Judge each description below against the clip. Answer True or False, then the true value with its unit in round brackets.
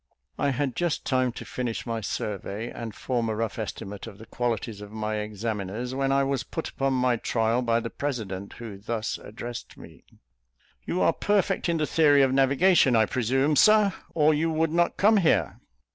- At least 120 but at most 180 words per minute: False (190 wpm)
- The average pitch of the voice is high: False (125 Hz)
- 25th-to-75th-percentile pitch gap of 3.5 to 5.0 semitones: True (4.6 semitones)